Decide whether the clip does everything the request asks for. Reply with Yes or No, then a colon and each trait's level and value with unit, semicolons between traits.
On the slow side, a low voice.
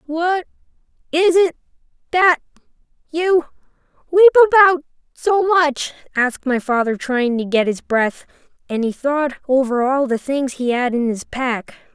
No: slow, 120 wpm; very high, 290 Hz